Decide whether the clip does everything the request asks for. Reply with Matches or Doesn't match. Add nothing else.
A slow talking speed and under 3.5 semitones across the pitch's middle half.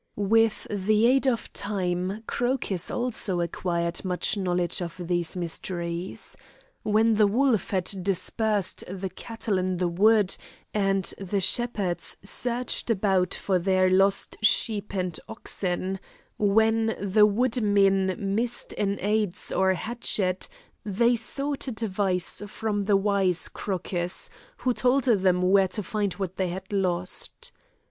Matches